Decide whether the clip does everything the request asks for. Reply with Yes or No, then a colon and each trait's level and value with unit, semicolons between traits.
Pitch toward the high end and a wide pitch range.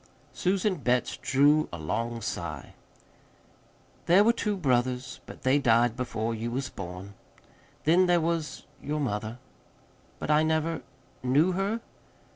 No: low, 135 Hz; wide, 6.1 semitones